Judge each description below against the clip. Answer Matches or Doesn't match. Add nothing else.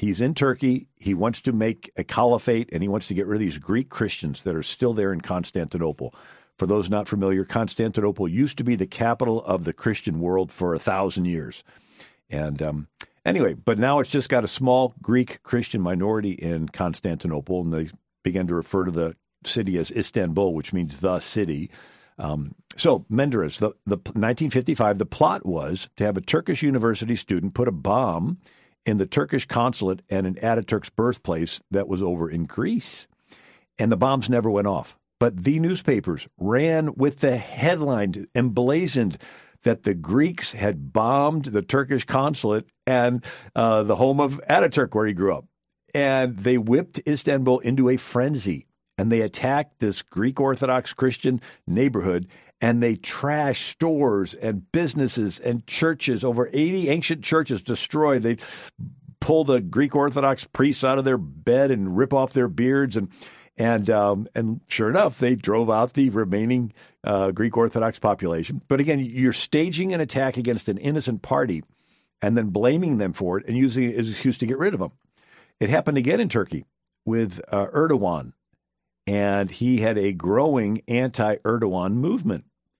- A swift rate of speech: Doesn't match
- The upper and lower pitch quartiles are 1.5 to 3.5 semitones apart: Doesn't match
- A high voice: Doesn't match